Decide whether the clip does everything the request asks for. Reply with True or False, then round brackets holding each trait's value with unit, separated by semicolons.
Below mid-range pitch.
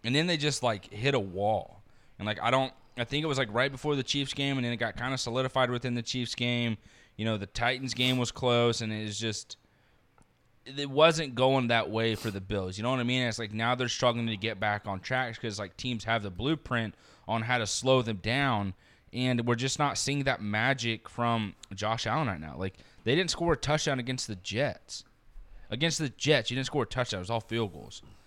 True (120 Hz)